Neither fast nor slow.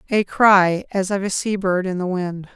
No: fast, 235 wpm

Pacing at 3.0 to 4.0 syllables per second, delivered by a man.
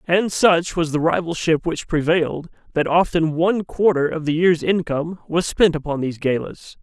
No: 5.0 syllables/s; male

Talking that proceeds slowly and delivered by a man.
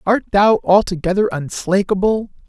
No: slow, 95 wpm; female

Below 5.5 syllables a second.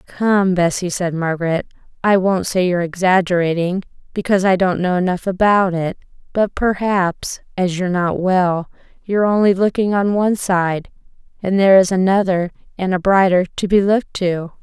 Yes: 5.1 syllables/s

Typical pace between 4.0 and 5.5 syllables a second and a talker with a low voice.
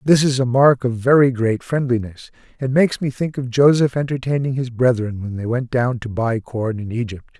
Yes: 5.3 syllables/s; low, 125 Hz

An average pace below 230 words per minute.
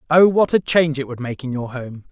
No: fast, 285 wpm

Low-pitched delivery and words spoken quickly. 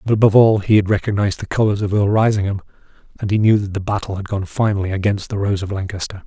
Yes: low, 100 Hz; fast, 240 wpm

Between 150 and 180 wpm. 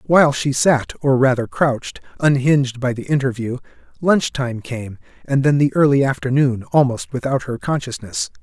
Yes: average, 155 wpm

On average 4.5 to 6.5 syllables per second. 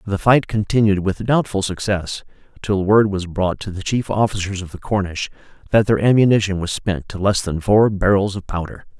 Yes: 5.1 syllables/s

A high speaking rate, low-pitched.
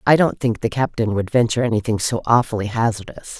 No: average, 195 wpm; low, 115 Hz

